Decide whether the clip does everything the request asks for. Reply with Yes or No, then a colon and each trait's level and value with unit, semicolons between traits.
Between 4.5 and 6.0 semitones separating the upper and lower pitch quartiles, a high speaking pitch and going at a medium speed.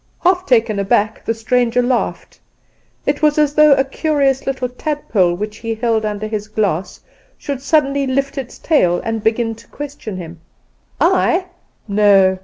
Yes: average, 4.8 semitones; high, 235 Hz; average, 155 wpm